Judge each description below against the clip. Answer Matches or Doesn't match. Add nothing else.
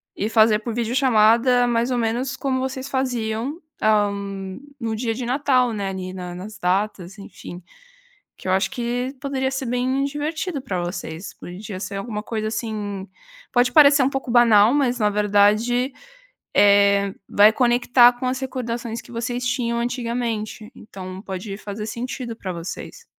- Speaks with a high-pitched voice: Matches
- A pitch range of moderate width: Matches